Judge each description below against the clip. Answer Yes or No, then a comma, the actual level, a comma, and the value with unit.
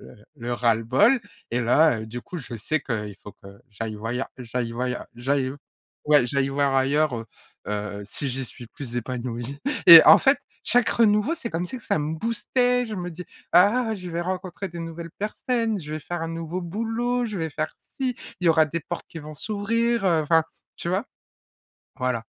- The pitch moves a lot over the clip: Yes, wide, 8.4 semitones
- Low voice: No, medium, 160 Hz